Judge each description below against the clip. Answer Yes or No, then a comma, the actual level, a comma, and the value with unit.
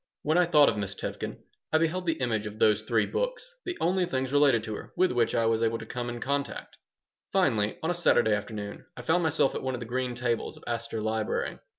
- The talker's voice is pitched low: Yes, low, 120 Hz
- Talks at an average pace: No, fast, 235 wpm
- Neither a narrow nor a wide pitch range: No, wide, 6.4 semitones